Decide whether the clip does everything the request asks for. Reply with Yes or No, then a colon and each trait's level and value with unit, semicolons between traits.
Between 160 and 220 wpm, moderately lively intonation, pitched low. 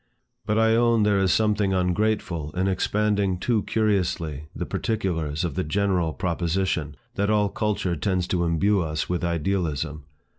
No: average, 150 wpm; average, 3.9 semitones; very low, 95 Hz